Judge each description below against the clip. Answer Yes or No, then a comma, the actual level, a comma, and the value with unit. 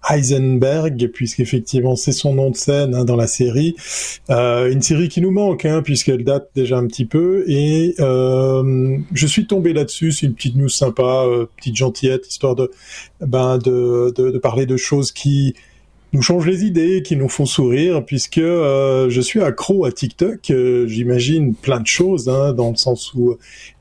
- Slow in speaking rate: No, average, 180 wpm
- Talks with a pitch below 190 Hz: Yes, low, 135 Hz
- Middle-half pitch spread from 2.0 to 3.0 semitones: No, average, 3.7 semitones